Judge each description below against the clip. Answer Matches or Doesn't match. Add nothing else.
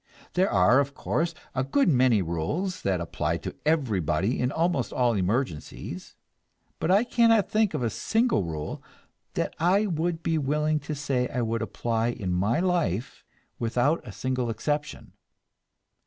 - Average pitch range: Doesn't match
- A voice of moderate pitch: Doesn't match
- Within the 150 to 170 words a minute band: Matches